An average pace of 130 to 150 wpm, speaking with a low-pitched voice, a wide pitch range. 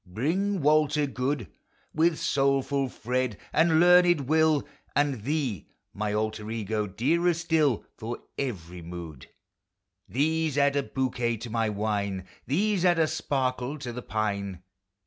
Yes: slow, 135 wpm; low, 130 Hz; wide, 6.2 semitones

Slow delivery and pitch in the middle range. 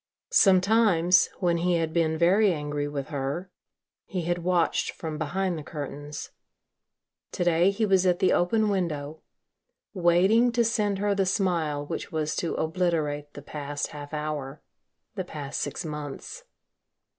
No: average, 145 wpm; medium, 170 Hz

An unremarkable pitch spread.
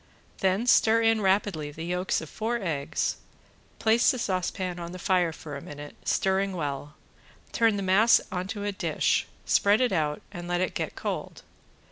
Yes: average, 3.7 semitones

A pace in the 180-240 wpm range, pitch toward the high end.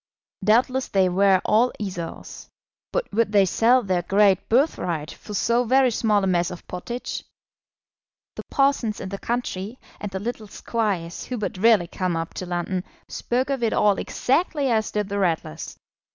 No: average, 165 wpm; high, 210 Hz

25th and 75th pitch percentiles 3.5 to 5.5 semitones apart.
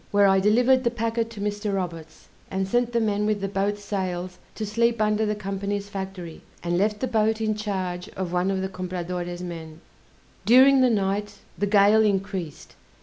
No: narrow, 2.6 semitones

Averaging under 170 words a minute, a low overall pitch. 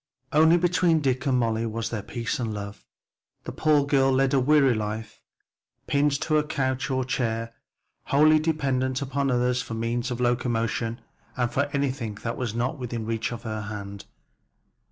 No: average, 175 wpm; low, 125 Hz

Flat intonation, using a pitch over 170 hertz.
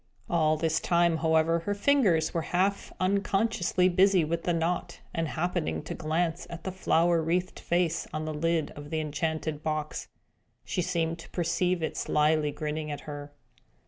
No: narrow, 2.1 semitones; medium, 165 Hz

